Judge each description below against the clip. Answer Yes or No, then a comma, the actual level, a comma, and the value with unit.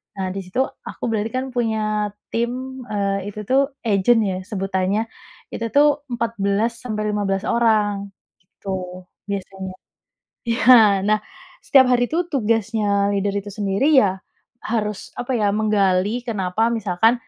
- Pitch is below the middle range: No, high, 210 Hz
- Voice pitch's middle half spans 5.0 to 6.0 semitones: No, average, 3.0 semitones